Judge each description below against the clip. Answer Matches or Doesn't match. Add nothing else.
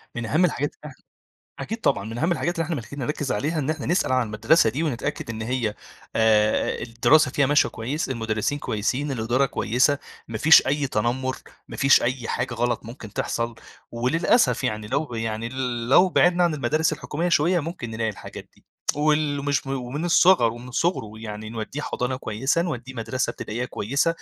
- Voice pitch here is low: Matches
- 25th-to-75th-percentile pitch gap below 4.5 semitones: Doesn't match